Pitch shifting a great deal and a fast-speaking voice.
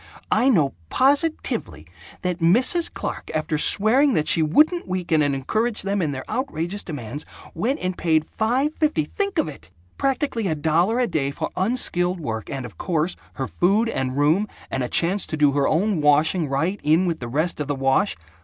No: wide, 6.8 semitones; average, 190 wpm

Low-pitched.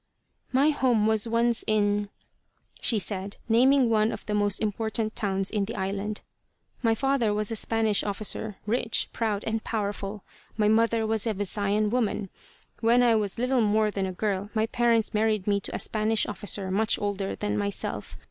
No: high, 215 Hz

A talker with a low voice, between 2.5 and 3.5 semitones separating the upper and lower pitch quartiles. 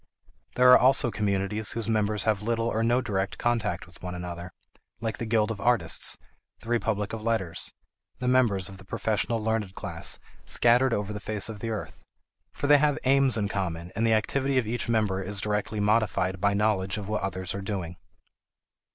Yes: low, 105 Hz; average, 2.9 semitones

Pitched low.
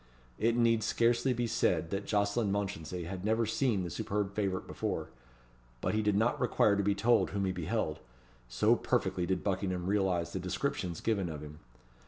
Yes: low, 100 Hz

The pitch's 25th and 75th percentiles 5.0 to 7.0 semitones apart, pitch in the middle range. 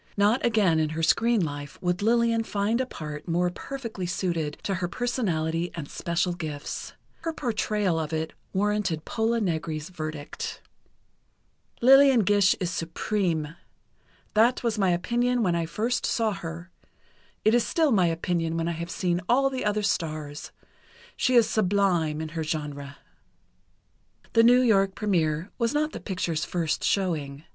Yes: wide, 5.6 semitones; medium, 180 Hz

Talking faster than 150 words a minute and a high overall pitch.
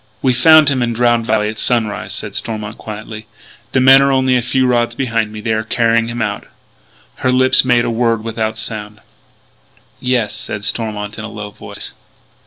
No: average, 190 wpm; low, 115 Hz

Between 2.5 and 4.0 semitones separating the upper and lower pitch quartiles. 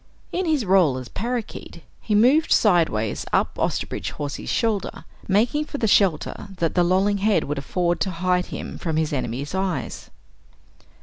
No: wide, 5.4 semitones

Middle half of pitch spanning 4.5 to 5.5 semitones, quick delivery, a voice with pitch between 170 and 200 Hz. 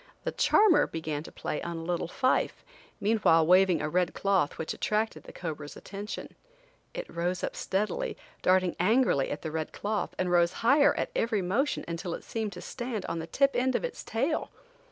No: average, 5.2 semitones; average, 190 wpm; medium, 185 Hz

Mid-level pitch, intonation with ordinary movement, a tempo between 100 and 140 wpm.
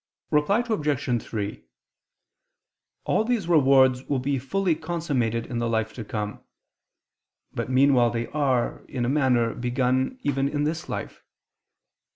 No: low, 130 Hz; average, 3.8 semitones; slow, 135 wpm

